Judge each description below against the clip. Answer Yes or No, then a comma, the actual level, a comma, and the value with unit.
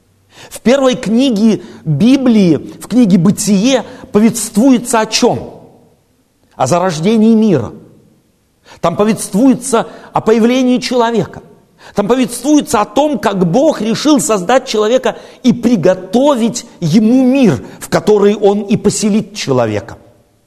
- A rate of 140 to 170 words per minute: No, slow, 110 wpm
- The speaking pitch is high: Yes, high, 220 Hz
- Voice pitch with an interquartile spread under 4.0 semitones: No, average, 4.8 semitones